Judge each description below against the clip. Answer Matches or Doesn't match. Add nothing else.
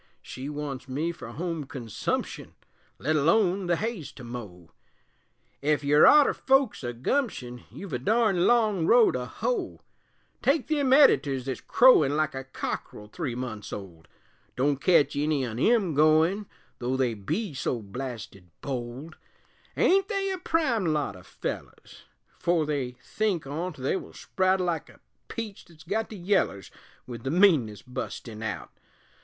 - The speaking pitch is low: Doesn't match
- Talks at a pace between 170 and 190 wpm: Doesn't match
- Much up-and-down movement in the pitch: Matches